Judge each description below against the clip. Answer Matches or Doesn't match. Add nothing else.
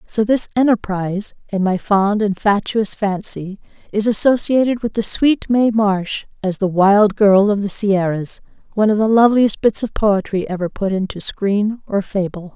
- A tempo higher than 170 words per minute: Doesn't match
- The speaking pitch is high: Matches